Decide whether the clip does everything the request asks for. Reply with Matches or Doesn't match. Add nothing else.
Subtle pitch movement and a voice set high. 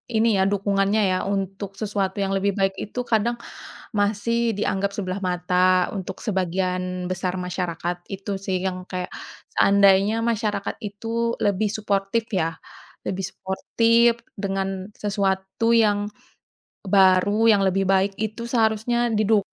Matches